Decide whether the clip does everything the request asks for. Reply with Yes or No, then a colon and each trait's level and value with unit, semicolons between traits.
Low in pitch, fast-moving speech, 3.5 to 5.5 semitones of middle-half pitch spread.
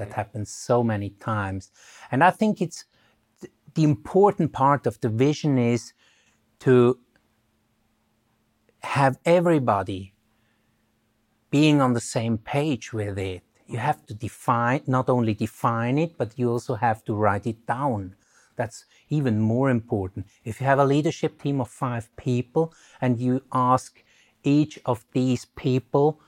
No: low, 125 Hz; average, 145 wpm; average, 4.3 semitones